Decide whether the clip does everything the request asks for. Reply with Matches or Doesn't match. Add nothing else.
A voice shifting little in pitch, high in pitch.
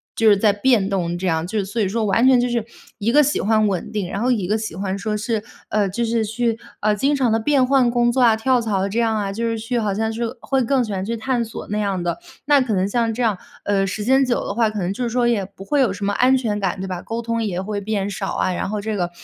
Doesn't match